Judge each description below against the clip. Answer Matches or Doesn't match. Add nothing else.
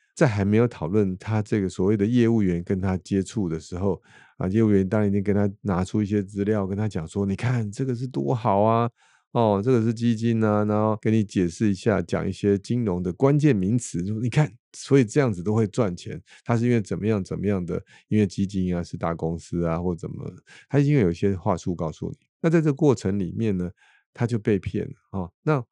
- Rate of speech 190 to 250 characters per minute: Doesn't match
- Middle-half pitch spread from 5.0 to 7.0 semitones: Doesn't match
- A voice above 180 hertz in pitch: Doesn't match